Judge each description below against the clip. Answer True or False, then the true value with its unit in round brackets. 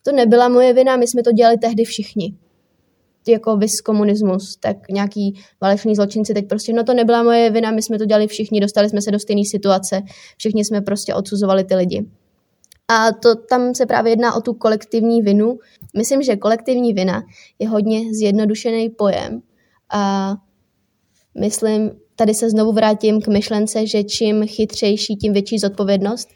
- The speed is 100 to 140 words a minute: False (165 wpm)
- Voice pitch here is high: True (215 Hz)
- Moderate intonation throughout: False (2.0 semitones)